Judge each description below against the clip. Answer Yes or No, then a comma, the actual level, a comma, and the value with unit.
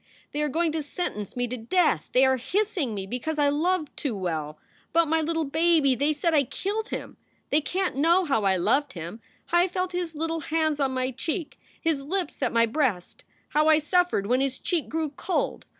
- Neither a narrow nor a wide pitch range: Yes, average, 4.7 semitones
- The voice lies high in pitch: Yes, very high, 300 Hz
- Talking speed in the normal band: No, fast, 215 wpm